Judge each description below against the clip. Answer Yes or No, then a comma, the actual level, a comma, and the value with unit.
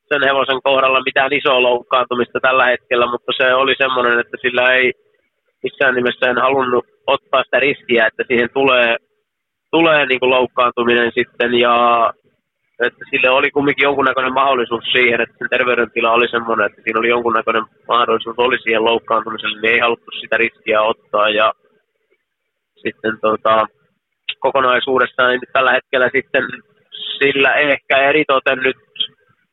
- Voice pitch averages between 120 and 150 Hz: Yes, low, 125 Hz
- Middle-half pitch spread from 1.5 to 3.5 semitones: Yes, narrow, 2.4 semitones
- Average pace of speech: Yes, average, 135 wpm